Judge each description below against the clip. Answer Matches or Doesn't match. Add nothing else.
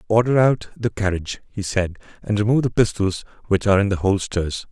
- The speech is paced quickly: Doesn't match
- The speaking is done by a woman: Doesn't match